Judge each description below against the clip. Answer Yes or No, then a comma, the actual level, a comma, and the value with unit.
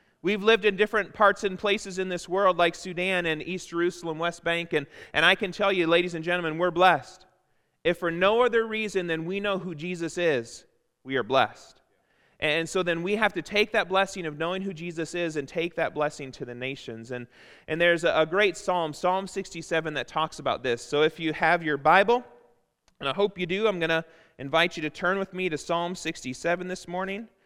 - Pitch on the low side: No, medium, 175 Hz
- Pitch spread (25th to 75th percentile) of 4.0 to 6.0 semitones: No, average, 2.9 semitones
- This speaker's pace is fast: Yes, fast, 220 wpm